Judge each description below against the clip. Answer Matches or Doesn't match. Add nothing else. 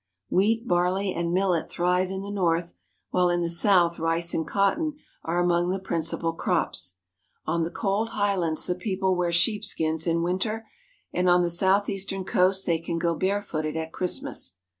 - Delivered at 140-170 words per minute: Matches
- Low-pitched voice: Doesn't match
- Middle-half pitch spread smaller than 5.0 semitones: Matches